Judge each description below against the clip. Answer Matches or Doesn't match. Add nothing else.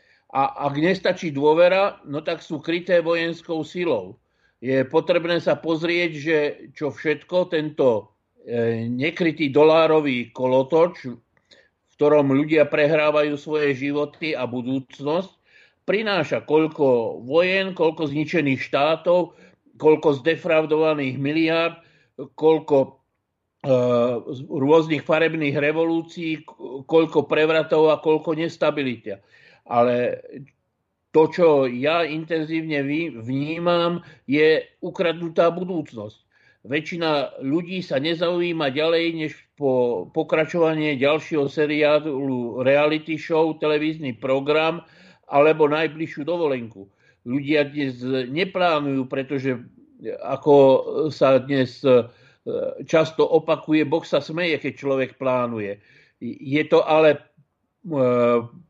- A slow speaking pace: Matches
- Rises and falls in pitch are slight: Doesn't match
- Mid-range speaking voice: Matches